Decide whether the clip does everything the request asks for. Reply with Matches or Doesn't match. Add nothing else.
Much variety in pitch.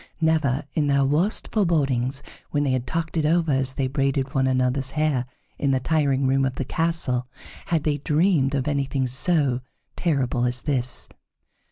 Doesn't match